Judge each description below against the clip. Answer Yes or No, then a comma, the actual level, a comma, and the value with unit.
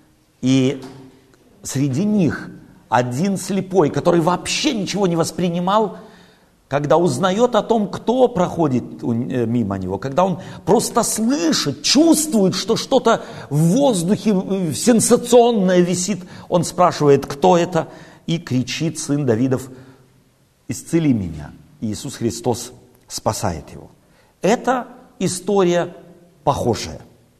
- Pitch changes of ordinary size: No, wide, 7.6 semitones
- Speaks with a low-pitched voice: No, medium, 175 Hz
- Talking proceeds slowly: Yes, slow, 100 wpm